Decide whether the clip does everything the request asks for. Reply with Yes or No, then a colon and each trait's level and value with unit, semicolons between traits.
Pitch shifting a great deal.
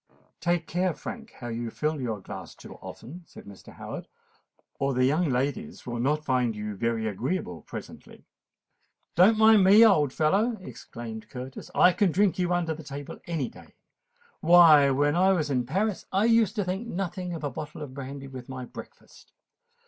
Yes: wide, 6.3 semitones